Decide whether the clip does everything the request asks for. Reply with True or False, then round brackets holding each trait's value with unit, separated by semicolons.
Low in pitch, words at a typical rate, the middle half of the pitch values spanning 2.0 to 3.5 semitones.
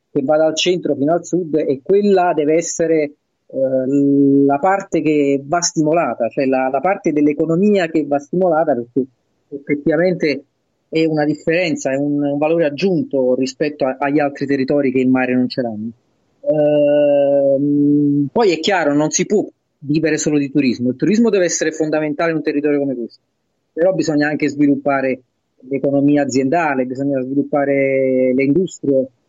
False (145 Hz; 155 wpm; 2.7 semitones)